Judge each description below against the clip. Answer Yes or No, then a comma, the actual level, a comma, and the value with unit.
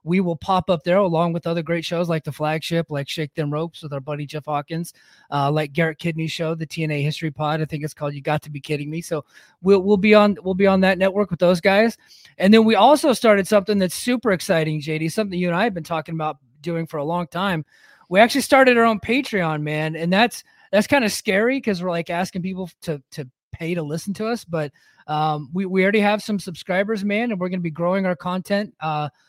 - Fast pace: Yes, fast, 245 wpm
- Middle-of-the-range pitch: Yes, medium, 175 Hz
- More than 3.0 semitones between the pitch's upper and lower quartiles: Yes, average, 4.2 semitones